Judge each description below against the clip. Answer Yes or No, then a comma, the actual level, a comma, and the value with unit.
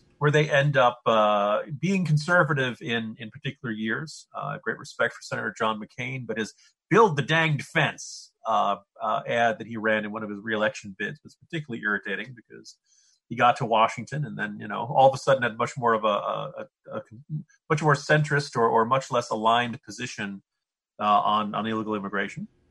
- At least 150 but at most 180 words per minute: No, average, 195 wpm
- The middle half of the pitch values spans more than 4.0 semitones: Yes, average, 4.7 semitones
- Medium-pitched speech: No, low, 120 Hz